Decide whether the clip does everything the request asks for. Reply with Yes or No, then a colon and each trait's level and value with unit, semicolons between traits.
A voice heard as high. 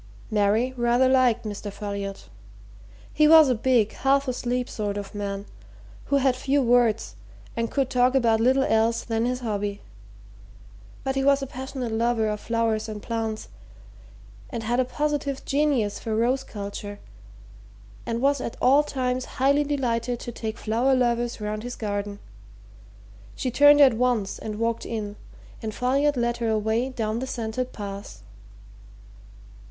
Yes: high, 235 Hz